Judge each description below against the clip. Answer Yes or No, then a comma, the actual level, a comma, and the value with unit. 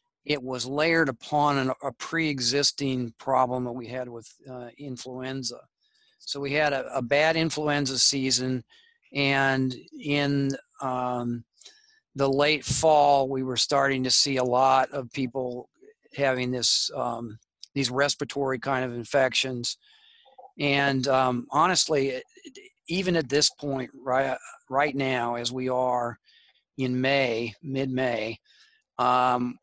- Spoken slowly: Yes, slow, 130 wpm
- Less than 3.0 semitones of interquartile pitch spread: Yes, narrow, 2.5 semitones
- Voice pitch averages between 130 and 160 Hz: Yes, low, 135 Hz